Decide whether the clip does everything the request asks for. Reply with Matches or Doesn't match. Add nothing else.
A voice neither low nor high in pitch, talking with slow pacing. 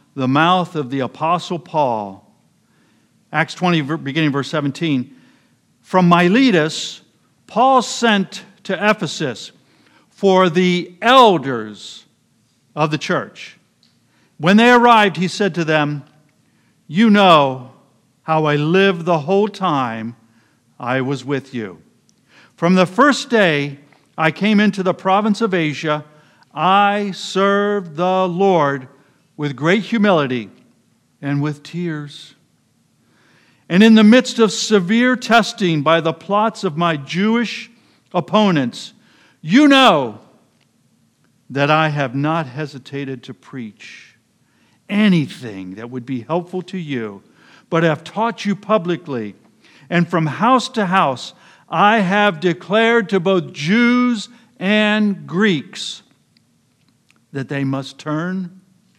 Matches